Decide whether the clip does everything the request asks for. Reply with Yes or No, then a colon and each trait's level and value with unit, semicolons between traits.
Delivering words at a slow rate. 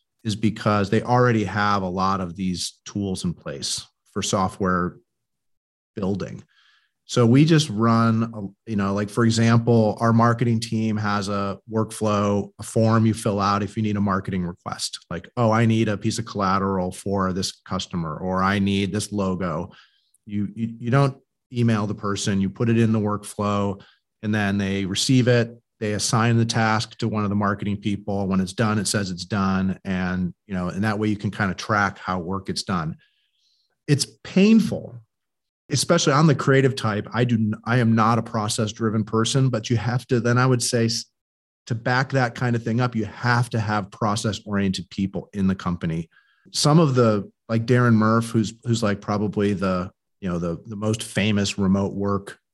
No: average, 190 wpm